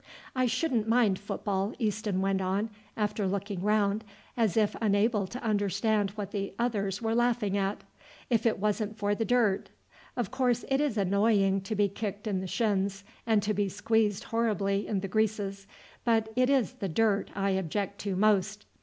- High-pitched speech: Yes, high, 210 Hz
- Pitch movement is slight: Yes, narrow, 2.2 semitones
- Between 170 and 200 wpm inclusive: Yes, average, 175 wpm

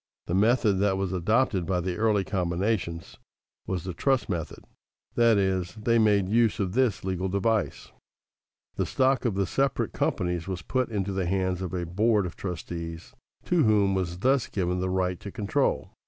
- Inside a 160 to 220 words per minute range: Yes, average, 175 wpm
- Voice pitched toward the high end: No, very low, 95 Hz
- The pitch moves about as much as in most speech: Yes, average, 3.4 semitones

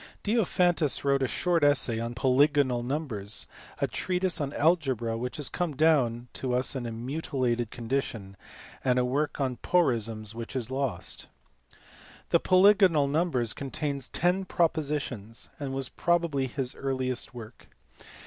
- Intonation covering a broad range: No, average, 4.4 semitones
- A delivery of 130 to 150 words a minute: Yes, average, 140 wpm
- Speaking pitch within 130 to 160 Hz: Yes, low, 135 Hz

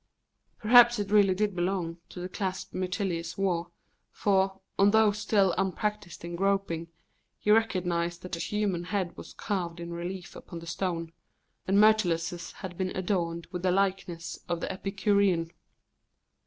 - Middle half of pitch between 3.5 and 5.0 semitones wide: No, average, 2.7 semitones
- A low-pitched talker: No, medium, 185 Hz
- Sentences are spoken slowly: No, average, 145 wpm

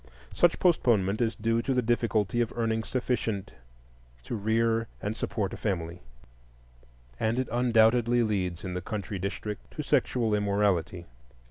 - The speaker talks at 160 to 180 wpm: No, average, 140 wpm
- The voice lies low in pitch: Yes, low, 110 Hz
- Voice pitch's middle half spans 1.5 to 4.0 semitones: Yes, average, 2.9 semitones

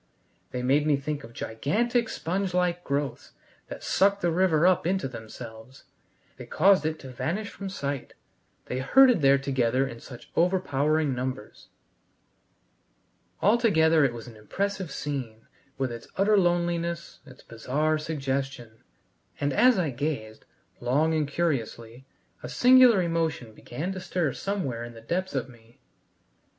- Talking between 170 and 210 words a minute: No, average, 140 wpm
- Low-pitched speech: No, medium, 150 Hz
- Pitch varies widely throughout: Yes, wide, 6.0 semitones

